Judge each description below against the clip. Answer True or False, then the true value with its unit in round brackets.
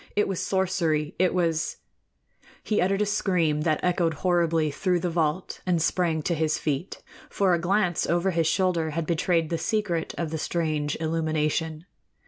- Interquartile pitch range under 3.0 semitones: True (2.5 semitones)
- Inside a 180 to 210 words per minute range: False (165 wpm)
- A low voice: False (170 Hz)